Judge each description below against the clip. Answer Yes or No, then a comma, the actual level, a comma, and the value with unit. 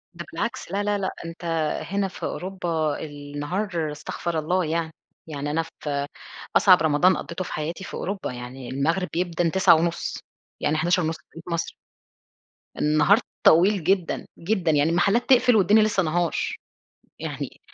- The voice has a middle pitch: Yes, medium, 170 Hz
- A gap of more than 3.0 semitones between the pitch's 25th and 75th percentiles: Yes, average, 3.6 semitones